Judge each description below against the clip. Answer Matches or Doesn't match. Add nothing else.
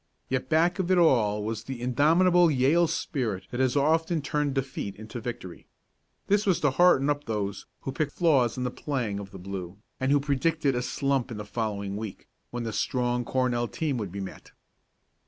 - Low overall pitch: Matches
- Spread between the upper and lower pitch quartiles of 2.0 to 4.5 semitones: Doesn't match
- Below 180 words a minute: Doesn't match